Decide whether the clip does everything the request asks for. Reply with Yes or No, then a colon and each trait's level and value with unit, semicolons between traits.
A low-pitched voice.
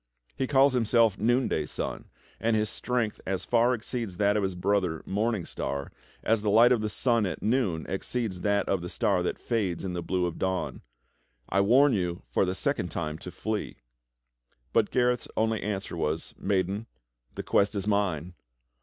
Yes: low, 100 Hz